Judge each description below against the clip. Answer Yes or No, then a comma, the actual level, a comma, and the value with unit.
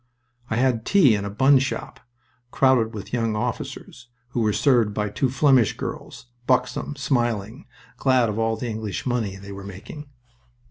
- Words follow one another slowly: No, average, 160 wpm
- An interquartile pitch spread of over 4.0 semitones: No, average, 3.5 semitones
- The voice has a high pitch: No, low, 120 Hz